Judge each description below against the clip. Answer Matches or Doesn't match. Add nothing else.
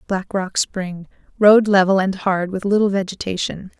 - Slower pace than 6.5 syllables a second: Matches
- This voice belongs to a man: Doesn't match